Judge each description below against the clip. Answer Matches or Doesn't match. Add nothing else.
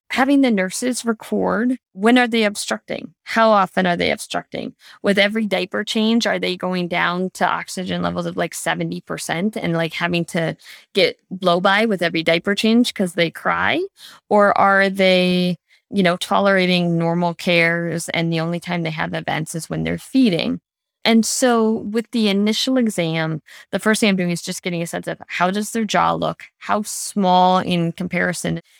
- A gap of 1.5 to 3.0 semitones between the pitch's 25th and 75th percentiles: Doesn't match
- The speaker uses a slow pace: Doesn't match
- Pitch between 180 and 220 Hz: Matches